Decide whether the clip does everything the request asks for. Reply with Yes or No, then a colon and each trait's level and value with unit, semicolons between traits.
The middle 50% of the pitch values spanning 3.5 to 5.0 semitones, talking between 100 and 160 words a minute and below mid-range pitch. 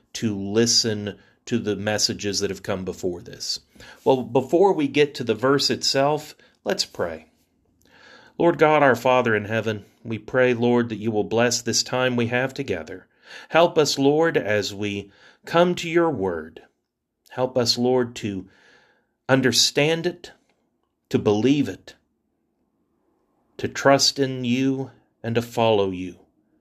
Yes: average, 4.2 semitones; average, 145 wpm; low, 120 Hz